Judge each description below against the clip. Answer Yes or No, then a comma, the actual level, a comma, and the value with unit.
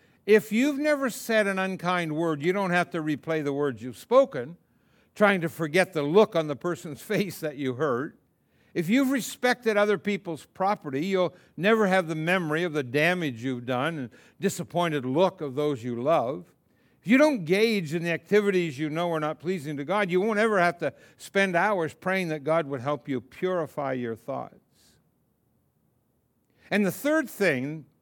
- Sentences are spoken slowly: No, average, 180 wpm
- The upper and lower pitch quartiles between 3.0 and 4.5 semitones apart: No, average, 4.9 semitones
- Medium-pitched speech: Yes, medium, 175 Hz